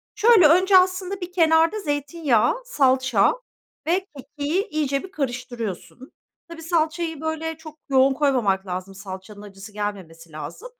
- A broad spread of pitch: Yes, wide, 8.1 semitones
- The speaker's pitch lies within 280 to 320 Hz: Yes, very high, 290 Hz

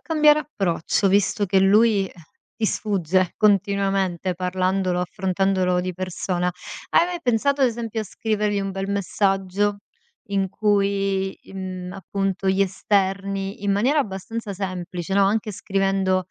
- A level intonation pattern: Yes, narrow, 1.7 semitones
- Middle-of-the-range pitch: No, high, 195 Hz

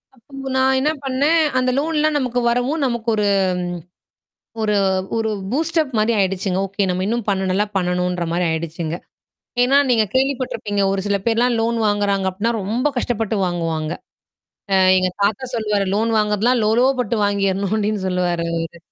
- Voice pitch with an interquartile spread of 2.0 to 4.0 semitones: No, average, 4.6 semitones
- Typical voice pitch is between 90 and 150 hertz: No, high, 215 Hz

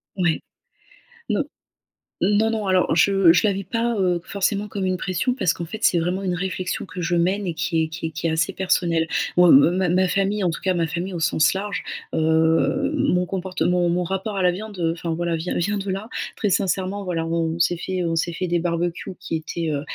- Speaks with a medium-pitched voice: Yes, medium, 180 Hz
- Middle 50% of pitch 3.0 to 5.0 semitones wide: No, narrow, 2.6 semitones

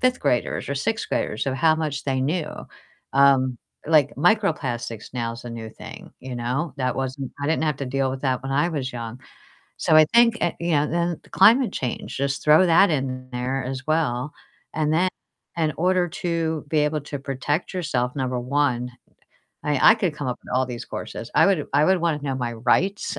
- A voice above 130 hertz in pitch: Yes, medium, 140 Hz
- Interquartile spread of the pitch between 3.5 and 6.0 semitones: Yes, average, 4.1 semitones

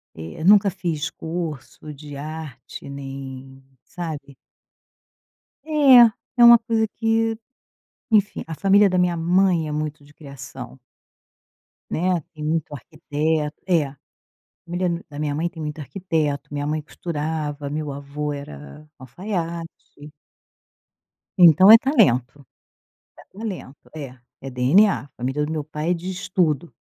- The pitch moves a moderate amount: Yes, average, 4.0 semitones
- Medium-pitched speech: Yes, medium, 155 Hz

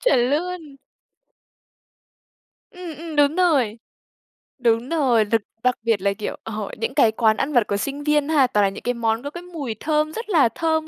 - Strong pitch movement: Yes, wide, 5.8 semitones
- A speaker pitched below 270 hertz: No, very high, 275 Hz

